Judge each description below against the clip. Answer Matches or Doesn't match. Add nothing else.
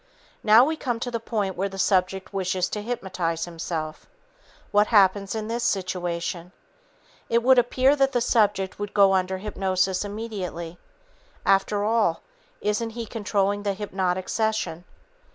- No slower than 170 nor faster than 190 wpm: Doesn't match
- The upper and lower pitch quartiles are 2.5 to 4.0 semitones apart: Matches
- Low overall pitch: Doesn't match